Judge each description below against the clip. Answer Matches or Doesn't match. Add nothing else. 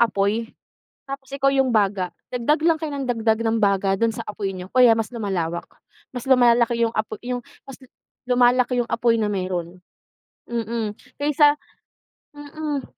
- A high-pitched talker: Matches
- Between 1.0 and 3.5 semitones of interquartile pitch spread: Doesn't match